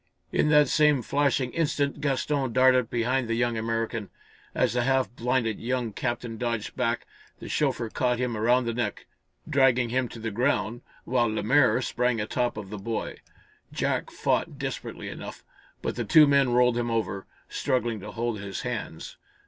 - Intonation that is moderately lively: No, narrow, 2.3 semitones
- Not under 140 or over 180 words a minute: Yes, average, 170 wpm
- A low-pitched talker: Yes, low, 120 Hz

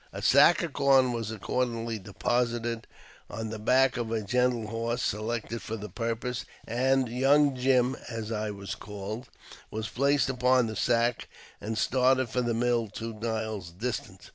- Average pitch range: No, narrow, 2.3 semitones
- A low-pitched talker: Yes, low, 115 Hz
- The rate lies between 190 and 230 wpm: No, average, 165 wpm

